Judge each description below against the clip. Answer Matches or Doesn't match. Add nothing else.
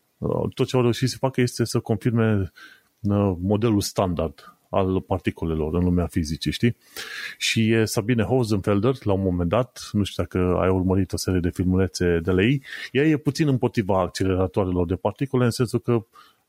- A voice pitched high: Doesn't match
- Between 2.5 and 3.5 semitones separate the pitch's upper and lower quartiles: Doesn't match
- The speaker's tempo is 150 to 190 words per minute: Matches